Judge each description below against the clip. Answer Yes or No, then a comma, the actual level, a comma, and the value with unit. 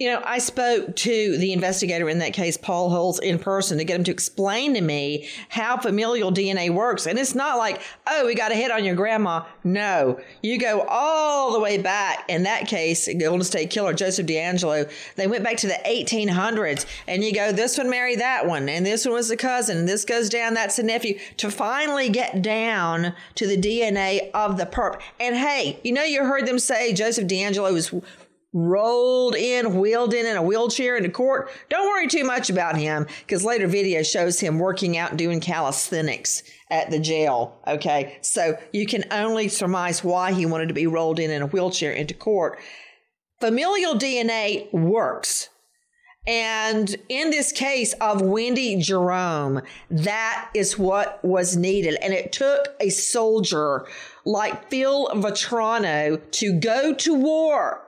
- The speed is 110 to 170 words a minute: No, average, 180 wpm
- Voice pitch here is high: Yes, high, 205 Hz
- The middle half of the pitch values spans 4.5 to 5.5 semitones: Yes, average, 5.0 semitones